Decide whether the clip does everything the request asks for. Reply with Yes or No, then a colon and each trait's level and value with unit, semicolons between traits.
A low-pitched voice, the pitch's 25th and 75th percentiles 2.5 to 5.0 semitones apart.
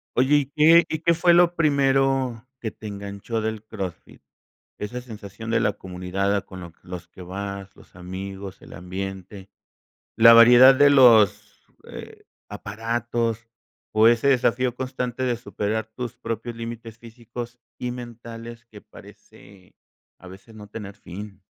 Yes: low, 115 Hz; average, 3.7 semitones